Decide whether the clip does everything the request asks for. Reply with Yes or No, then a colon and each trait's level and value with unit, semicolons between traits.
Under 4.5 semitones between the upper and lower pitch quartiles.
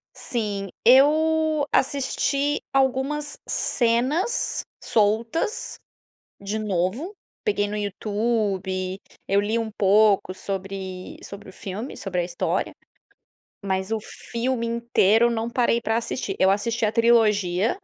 Yes: average, 4.1 semitones